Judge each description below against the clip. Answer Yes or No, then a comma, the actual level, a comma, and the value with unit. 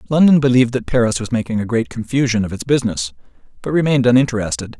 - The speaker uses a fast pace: No, average, 190 wpm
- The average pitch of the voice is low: Yes, low, 125 Hz